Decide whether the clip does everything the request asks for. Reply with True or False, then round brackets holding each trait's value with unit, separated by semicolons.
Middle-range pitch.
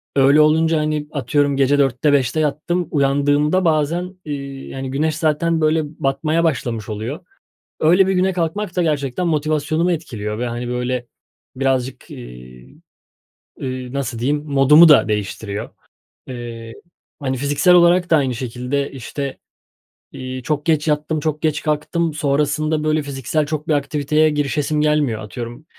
True (145 Hz)